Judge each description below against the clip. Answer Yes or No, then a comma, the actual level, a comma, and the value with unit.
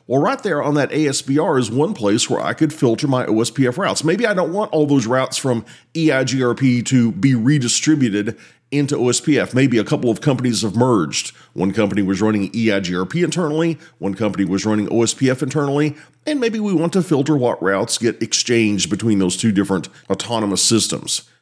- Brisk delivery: No, average, 180 wpm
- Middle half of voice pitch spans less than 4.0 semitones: No, average, 5.3 semitones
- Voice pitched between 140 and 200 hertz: No, low, 125 Hz